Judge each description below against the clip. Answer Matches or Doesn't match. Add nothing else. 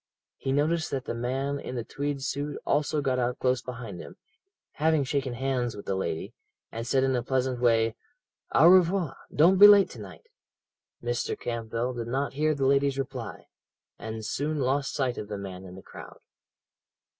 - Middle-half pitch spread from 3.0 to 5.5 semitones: Matches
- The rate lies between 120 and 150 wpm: Doesn't match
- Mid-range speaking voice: Doesn't match